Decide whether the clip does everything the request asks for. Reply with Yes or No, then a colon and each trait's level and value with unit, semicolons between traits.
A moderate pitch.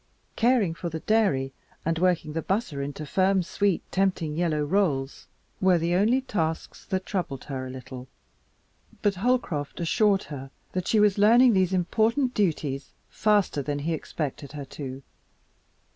Yes: medium, 175 Hz